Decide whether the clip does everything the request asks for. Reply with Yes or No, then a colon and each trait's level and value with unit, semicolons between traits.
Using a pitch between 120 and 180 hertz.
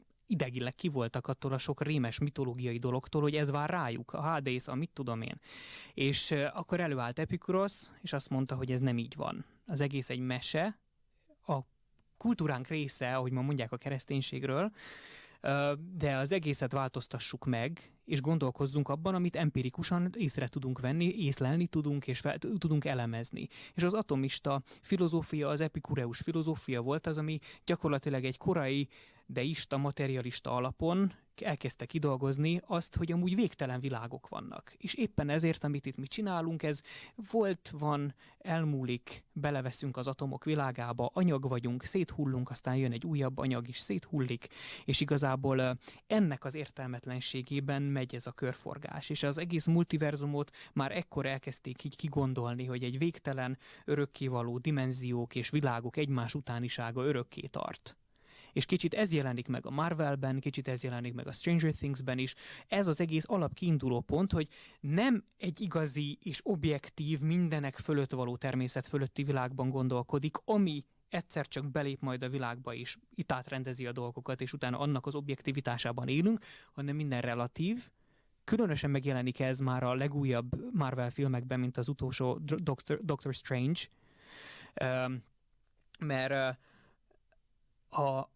Yes: medium, 140 Hz